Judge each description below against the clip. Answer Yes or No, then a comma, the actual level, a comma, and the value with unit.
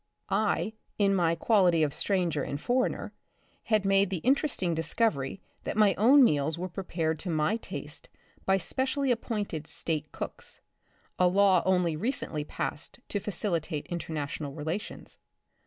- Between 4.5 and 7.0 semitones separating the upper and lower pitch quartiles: Yes, average, 4.8 semitones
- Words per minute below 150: Yes, average, 140 wpm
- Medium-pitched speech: Yes, medium, 180 Hz